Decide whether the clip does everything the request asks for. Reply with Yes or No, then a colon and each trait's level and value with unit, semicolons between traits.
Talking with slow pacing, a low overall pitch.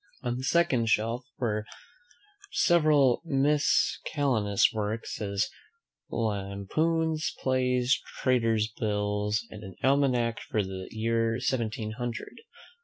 Yes: slow, 100 wpm; low, 115 Hz